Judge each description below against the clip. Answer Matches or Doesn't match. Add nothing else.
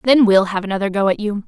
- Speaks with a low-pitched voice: Doesn't match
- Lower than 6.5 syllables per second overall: Doesn't match